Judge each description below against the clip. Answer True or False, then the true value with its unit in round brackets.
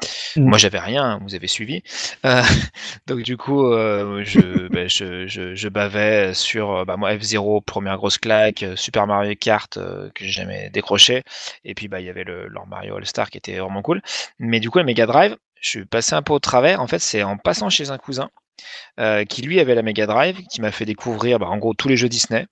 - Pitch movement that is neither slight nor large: True (3.4 semitones)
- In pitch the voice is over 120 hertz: False (110 Hz)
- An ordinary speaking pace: False (225 wpm)